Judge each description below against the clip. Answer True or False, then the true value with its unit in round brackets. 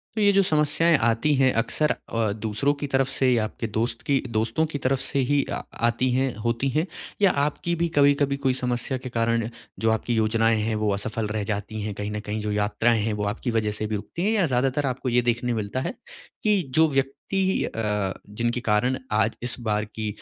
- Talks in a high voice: False (120 Hz)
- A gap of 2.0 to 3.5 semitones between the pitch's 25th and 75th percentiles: False (4.2 semitones)